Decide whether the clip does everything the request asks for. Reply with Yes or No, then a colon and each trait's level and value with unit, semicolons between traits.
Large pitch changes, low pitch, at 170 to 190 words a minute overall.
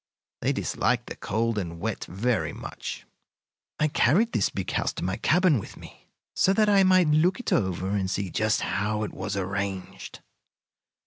Yes: wide, 8.9 semitones; low, 110 Hz; average, 175 wpm